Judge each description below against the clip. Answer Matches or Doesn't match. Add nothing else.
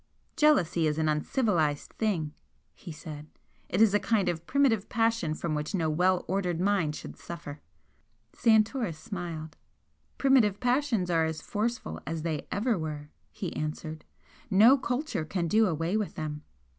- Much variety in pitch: Matches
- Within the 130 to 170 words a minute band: Matches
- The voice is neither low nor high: Matches